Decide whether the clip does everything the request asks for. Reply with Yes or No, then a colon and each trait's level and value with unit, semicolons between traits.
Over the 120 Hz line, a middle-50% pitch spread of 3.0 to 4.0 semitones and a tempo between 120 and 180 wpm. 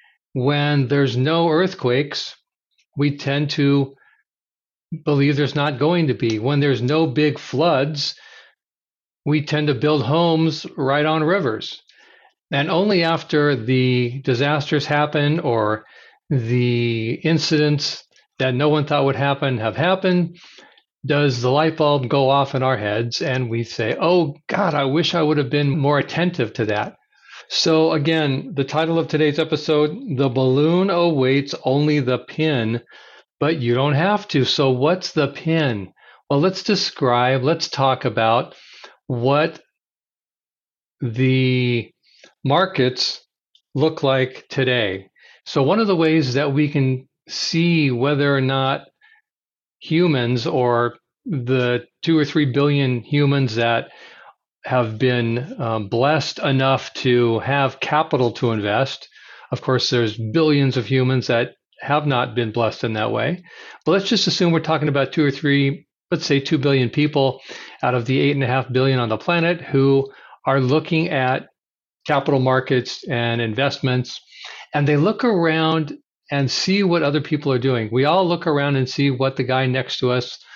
Yes: medium, 140 Hz; average, 3.4 semitones; average, 150 wpm